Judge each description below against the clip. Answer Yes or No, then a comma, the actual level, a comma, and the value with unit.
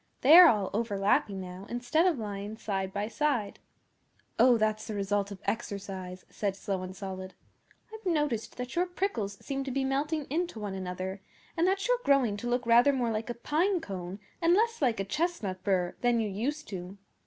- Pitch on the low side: No, high, 225 Hz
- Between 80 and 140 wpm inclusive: No, average, 190 wpm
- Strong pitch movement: Yes, wide, 7.0 semitones